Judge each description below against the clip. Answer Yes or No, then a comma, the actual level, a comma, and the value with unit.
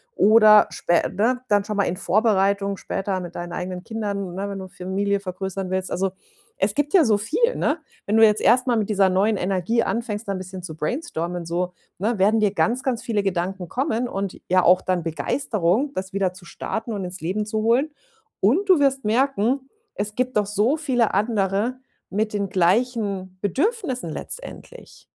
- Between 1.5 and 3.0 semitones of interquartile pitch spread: No, average, 3.9 semitones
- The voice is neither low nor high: No, high, 205 Hz